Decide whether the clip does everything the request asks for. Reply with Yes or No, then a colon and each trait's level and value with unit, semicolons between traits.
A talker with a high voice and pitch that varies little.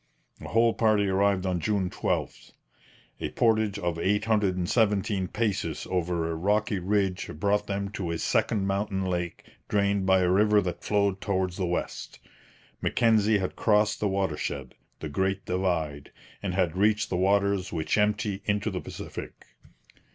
No: low, 100 Hz; narrow, 2.3 semitones